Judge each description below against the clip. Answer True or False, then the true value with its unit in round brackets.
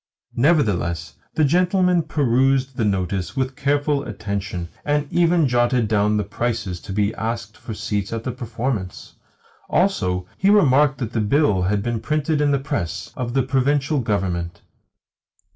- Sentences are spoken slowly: False (150 wpm)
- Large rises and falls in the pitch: True (5.9 semitones)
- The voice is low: True (120 Hz)